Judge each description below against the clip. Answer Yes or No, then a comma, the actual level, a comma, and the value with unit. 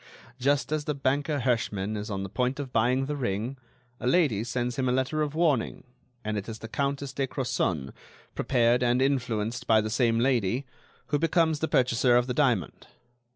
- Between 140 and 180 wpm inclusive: No, average, 190 wpm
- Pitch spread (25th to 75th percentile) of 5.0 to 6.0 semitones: No, average, 3.5 semitones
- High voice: No, low, 125 Hz